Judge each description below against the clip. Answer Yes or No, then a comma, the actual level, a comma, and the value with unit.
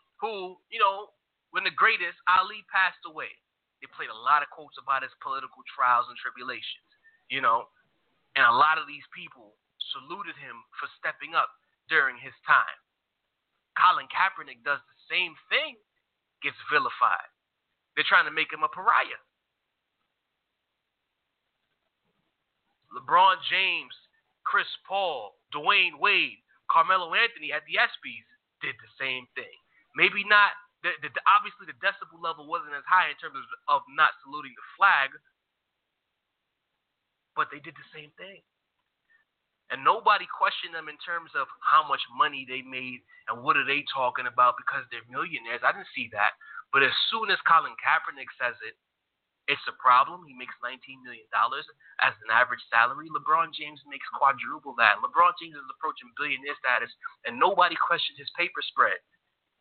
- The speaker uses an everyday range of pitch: No, wide, 7.6 semitones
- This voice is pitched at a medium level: Yes, medium, 180 Hz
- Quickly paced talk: No, average, 155 wpm